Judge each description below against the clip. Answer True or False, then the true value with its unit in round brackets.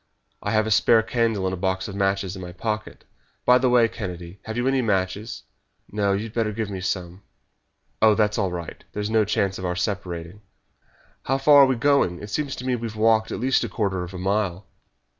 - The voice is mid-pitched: False (105 Hz)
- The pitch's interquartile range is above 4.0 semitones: False (3.3 semitones)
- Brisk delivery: True (235 wpm)